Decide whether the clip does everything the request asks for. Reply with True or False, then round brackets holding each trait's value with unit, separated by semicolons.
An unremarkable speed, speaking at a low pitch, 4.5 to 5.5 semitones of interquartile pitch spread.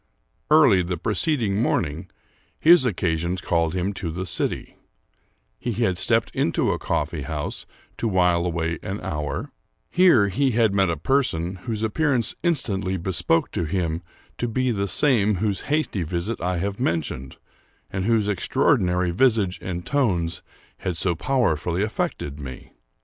True (145 wpm; 95 Hz; 5.1 semitones)